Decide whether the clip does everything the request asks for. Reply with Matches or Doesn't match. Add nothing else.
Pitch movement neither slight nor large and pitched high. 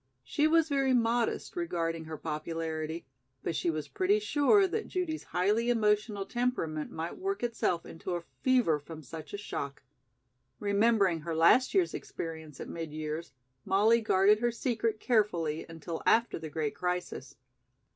Doesn't match